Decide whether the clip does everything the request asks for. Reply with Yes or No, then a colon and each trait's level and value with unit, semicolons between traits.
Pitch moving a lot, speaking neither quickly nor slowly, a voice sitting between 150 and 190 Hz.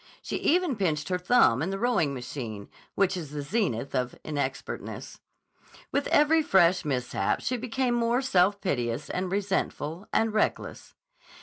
Yes: wide, 8.5 semitones; average, 145 wpm; medium, 185 Hz